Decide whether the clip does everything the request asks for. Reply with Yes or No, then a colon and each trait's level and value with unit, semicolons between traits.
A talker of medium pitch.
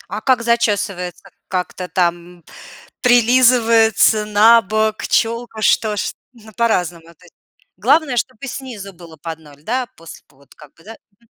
No: high, 215 Hz